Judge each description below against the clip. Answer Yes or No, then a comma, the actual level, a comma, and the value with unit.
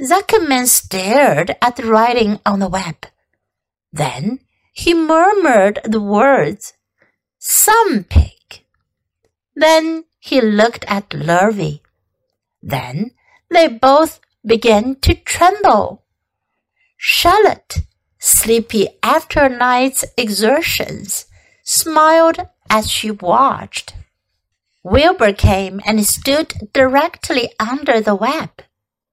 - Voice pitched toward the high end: Yes, high, 235 Hz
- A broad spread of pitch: Yes, wide, 8.0 semitones